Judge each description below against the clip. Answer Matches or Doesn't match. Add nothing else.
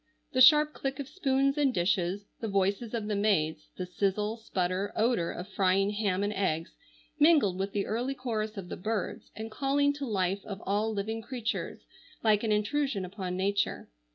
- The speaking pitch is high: Matches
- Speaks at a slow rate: Doesn't match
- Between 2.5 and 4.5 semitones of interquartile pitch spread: Matches